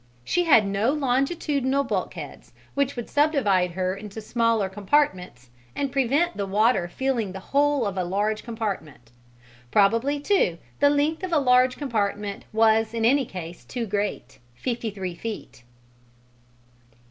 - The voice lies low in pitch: No, high, 225 Hz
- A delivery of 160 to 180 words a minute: No, average, 140 wpm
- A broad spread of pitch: Yes, wide, 5.9 semitones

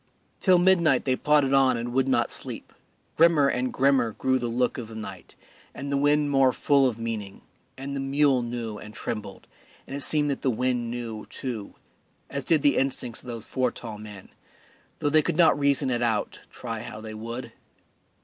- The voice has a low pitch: Yes, low, 130 Hz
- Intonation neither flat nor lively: Yes, average, 3.3 semitones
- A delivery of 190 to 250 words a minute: Yes, average, 195 wpm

